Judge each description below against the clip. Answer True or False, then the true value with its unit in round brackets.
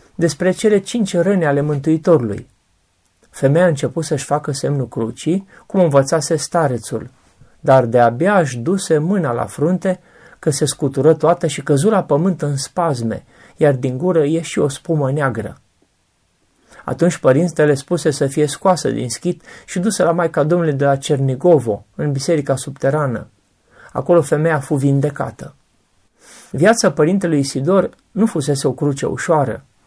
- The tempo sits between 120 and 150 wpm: True (145 wpm)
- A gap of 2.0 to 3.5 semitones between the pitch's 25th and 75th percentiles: False (3.9 semitones)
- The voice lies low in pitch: False (155 Hz)